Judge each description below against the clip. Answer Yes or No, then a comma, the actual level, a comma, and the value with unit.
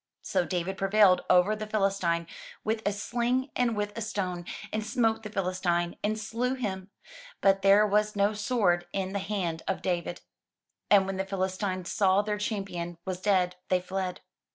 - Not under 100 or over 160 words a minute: No, average, 170 wpm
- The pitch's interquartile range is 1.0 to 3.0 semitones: Yes, narrow, 2.5 semitones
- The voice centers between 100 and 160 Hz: No, high, 195 Hz